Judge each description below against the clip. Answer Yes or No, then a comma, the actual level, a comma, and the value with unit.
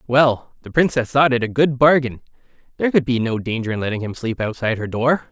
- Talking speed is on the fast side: Yes, fast, 225 wpm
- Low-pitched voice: Yes, low, 125 Hz